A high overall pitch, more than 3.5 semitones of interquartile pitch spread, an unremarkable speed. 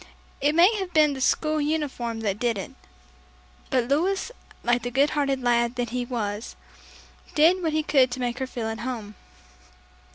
Yes: very high, 255 Hz; average, 4.3 semitones; average, 175 wpm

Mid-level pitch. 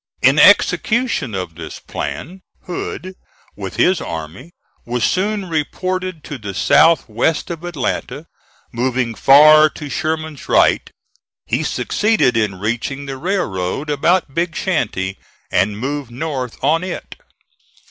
Yes: medium, 145 Hz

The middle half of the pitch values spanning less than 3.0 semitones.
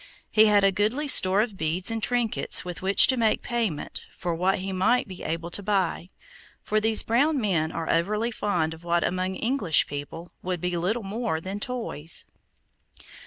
No: average, 4.4 semitones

